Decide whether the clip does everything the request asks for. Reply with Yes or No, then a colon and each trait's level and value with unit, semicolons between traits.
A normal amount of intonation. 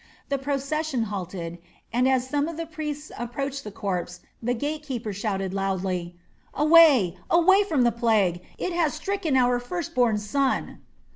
No: wide, 6.9 semitones